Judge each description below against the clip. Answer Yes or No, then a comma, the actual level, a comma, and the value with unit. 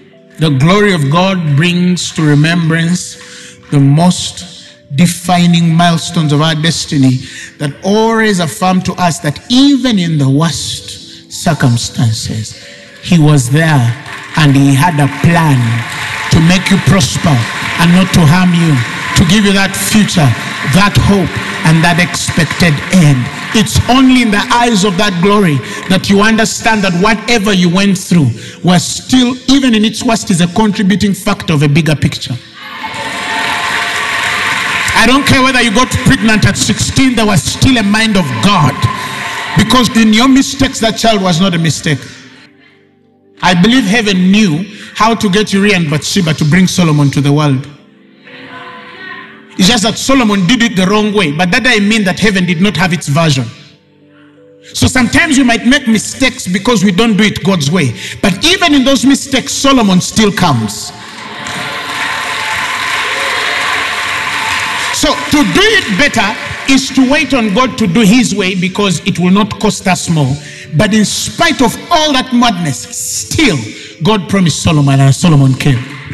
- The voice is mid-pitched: Yes, medium, 180 Hz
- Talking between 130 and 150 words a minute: No, average, 160 wpm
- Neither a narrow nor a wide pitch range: No, wide, 6.6 semitones